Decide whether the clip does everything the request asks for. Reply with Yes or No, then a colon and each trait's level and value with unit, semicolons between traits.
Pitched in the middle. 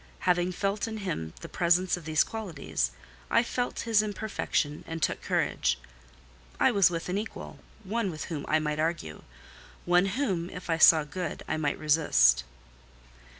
Yes: medium, 175 Hz